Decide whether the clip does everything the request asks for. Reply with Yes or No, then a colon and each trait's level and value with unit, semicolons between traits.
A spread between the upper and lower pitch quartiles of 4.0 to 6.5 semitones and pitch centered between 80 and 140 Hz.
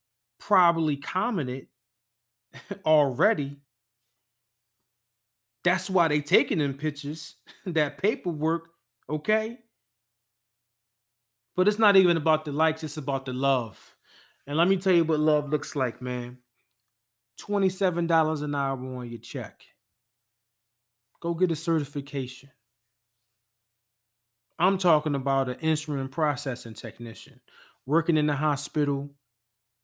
Yes: average, 5.2 semitones; low, 135 Hz